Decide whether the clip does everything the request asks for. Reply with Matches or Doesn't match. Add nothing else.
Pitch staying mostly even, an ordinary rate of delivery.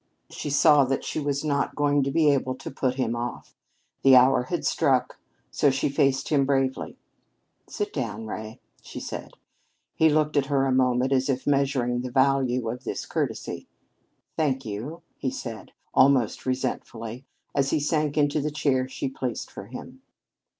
Matches